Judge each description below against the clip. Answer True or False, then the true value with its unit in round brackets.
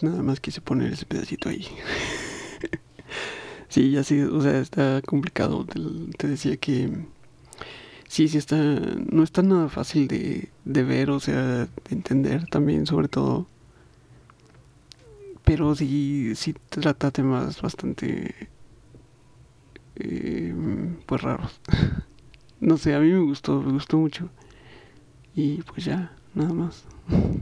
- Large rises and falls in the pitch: False (2.8 semitones)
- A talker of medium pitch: True (145 Hz)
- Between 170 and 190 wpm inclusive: False (125 wpm)